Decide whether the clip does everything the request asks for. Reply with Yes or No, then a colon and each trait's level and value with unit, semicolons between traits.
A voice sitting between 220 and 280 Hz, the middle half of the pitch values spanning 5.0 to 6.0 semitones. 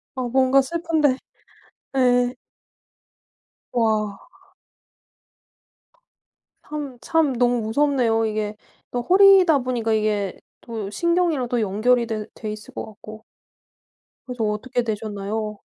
No: high, 240 Hz; average, 3.8 semitones